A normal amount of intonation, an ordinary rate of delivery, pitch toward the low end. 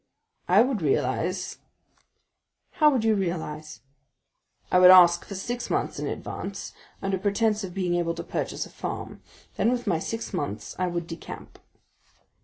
No: average, 4.1 semitones; average, 155 wpm; medium, 185 Hz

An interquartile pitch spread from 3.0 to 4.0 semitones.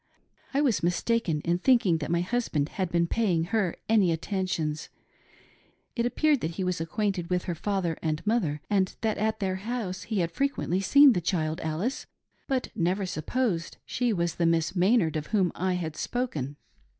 No: average, 5.0 semitones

